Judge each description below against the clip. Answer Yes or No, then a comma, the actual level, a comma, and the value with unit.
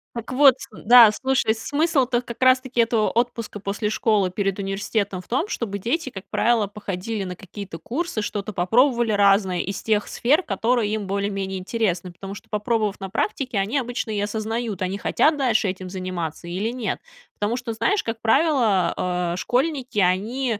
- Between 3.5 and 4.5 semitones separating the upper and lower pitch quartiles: Yes, average, 3.8 semitones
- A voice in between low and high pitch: No, high, 215 Hz